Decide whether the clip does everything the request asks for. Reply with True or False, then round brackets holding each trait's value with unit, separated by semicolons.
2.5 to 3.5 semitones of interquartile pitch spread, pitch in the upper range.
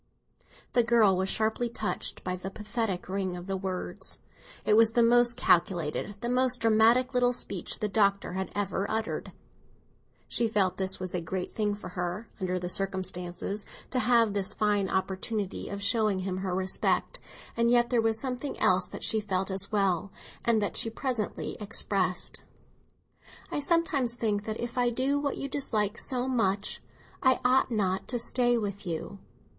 False (4.0 semitones; 210 Hz)